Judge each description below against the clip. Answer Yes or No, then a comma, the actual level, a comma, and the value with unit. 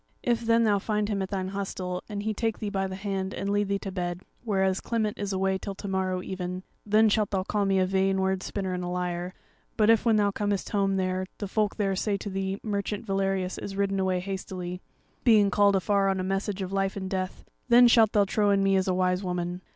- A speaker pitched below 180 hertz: No, high, 195 Hz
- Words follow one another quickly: Yes, fast, 240 wpm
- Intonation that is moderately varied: No, narrow, 1.6 semitones